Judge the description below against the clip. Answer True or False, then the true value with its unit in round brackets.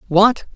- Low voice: False (205 Hz)